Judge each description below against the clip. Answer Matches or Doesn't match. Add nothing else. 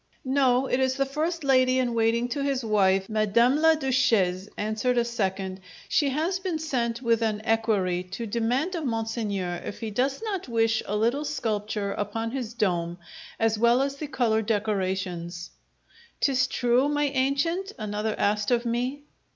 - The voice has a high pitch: Matches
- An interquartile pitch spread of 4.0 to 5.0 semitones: Matches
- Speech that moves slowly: Doesn't match